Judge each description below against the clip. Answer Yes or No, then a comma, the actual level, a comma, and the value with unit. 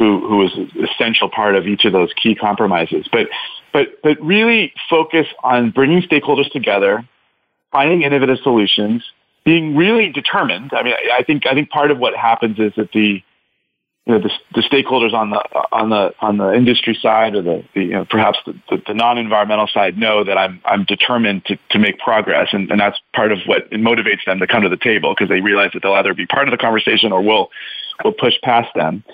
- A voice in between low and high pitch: No, low, 115 Hz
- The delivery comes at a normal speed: No, fast, 215 wpm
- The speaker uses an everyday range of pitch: No, wide, 5.8 semitones